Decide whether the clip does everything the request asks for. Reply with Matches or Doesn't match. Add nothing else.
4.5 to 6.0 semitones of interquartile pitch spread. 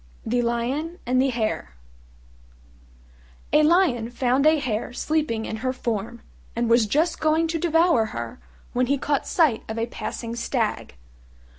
Matches